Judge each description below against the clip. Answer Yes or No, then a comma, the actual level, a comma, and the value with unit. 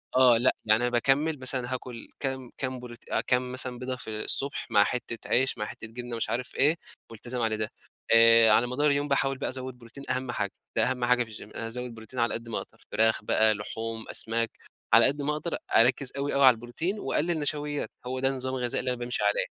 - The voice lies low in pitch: Yes, low, 125 Hz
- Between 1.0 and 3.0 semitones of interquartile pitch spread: Yes, narrow, 2.5 semitones